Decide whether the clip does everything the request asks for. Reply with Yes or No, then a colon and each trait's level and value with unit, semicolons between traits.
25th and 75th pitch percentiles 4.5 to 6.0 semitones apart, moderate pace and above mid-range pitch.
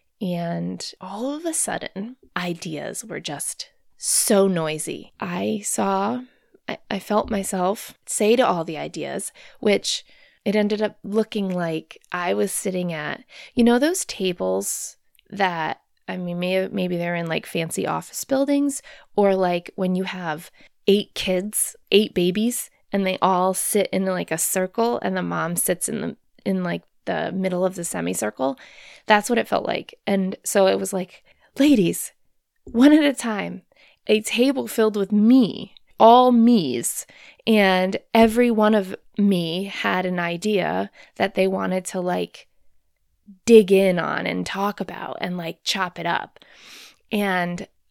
No: average, 3.7 semitones; average, 155 wpm; high, 195 Hz